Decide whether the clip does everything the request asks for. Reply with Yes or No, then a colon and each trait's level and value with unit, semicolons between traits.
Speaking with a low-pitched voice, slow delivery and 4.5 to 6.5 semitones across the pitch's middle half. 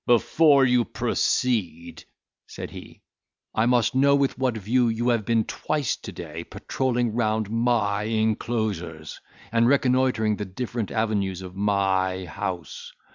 No: low, 110 Hz; slow, 130 wpm; average, 3.7 semitones